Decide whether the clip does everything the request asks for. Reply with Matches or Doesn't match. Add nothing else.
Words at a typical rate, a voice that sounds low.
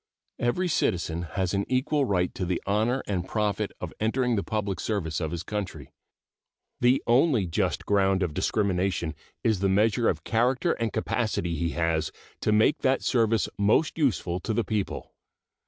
Matches